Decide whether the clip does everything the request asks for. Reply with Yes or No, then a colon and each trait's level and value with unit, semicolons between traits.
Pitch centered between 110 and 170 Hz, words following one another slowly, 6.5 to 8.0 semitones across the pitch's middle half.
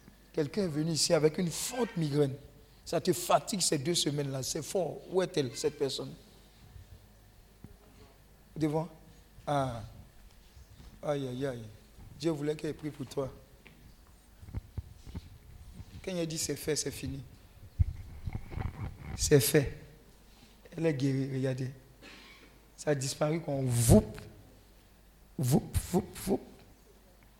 Yes: low, 135 Hz; slow, 115 wpm; wide, 6.9 semitones